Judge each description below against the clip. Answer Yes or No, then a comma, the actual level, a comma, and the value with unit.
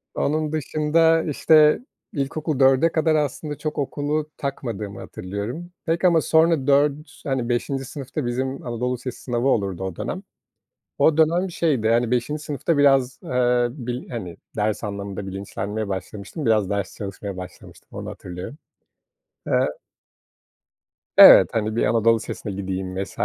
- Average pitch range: No, wide, 6.3 semitones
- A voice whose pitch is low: Yes, low, 125 Hz